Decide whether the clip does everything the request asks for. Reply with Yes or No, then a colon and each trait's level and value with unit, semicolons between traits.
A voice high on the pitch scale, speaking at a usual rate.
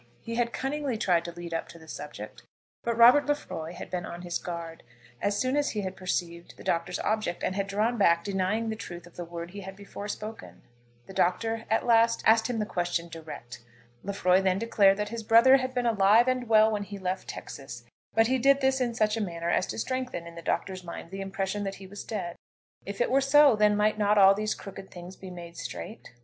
No: high, 200 Hz; fast, 230 wpm